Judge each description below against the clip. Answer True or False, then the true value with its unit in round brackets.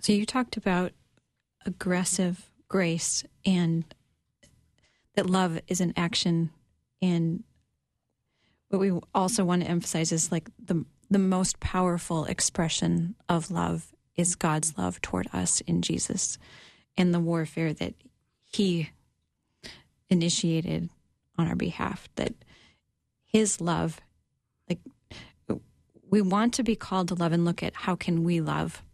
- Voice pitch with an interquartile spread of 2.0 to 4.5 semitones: True (2.6 semitones)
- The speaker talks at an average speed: False (130 wpm)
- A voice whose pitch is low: False (175 Hz)